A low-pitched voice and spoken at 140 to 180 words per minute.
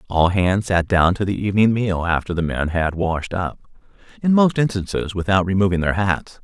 No: very low, 95 Hz; average, 195 wpm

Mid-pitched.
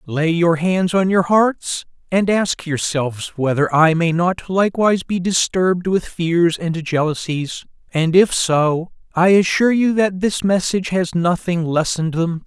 Yes: medium, 175 Hz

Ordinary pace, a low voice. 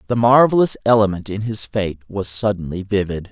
Yes: average, 165 wpm; low, 105 Hz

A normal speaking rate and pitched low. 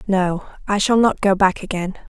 No: average, 195 wpm; high, 195 Hz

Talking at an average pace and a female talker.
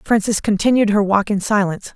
Yes: average, 185 wpm; female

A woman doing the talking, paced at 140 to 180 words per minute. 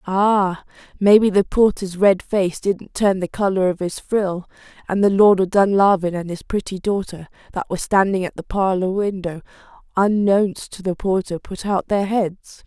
Yes: female; average, 175 wpm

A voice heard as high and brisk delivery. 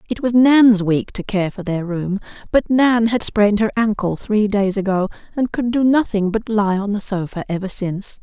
Yes: high, 210 Hz; fast, 210 wpm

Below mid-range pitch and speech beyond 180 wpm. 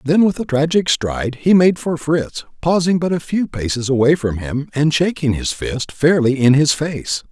No: medium, 150 Hz; fast, 205 wpm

